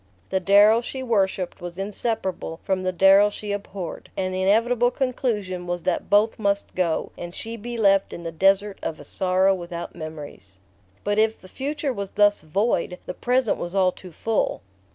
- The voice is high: Yes, high, 195 Hz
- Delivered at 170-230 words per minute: Yes, average, 180 wpm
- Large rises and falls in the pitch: No, average, 3.2 semitones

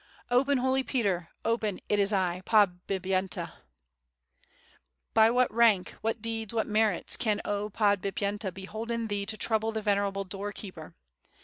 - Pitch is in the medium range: No, high, 205 Hz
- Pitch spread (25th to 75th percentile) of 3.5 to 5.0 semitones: No, narrow, 2.5 semitones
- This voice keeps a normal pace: Yes, average, 150 wpm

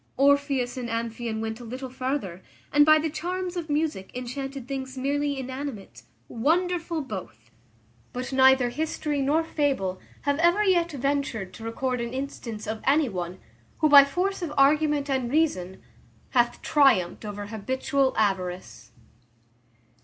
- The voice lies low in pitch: No, very high, 265 Hz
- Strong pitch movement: No, average, 4.5 semitones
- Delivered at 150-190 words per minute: No, average, 140 wpm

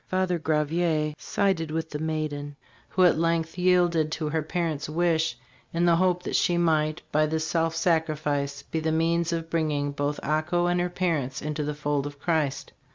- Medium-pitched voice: Yes, medium, 160 Hz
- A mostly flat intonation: Yes, narrow, 2.1 semitones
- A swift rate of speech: No, average, 185 wpm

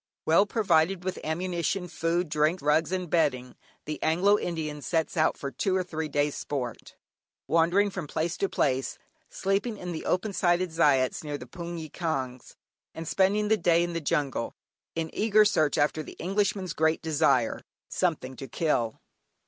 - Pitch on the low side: No, medium, 165 Hz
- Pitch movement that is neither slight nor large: Yes, average, 3.6 semitones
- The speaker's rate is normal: Yes, average, 165 wpm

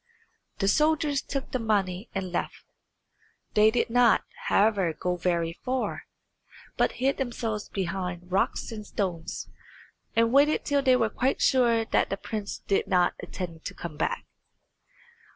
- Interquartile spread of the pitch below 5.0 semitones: No, wide, 5.6 semitones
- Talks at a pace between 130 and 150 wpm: Yes, average, 145 wpm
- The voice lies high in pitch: Yes, high, 210 Hz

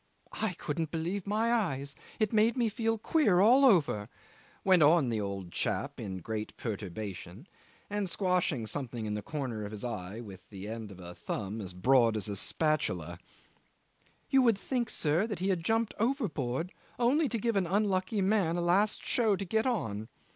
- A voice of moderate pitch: Yes, medium, 165 Hz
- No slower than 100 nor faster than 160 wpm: No, average, 175 wpm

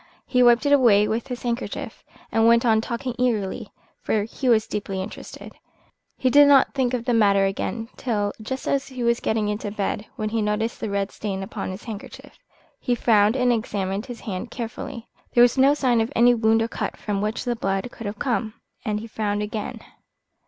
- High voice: Yes, high, 225 Hz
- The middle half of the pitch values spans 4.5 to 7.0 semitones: No, average, 2.8 semitones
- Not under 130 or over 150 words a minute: No, average, 200 wpm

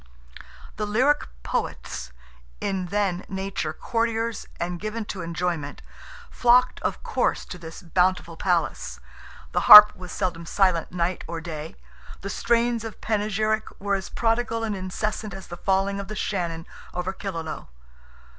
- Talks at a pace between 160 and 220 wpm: No, average, 140 wpm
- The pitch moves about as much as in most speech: Yes, average, 3.7 semitones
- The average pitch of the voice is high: Yes, high, 195 Hz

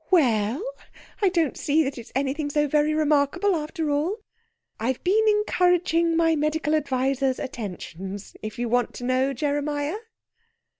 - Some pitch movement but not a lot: Yes, average, 3.9 semitones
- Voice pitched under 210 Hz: No, very high, 295 Hz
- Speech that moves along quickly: No, average, 145 wpm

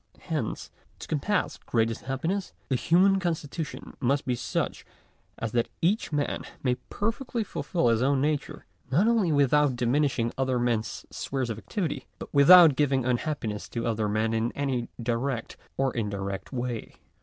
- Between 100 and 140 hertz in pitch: Yes, low, 135 Hz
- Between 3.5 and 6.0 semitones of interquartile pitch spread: Yes, average, 4.7 semitones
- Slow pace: No, average, 150 wpm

